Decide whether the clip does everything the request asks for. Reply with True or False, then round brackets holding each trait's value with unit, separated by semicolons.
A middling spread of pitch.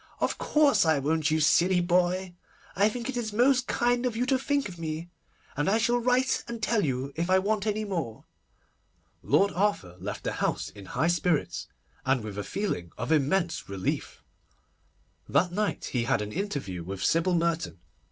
False (7.0 semitones)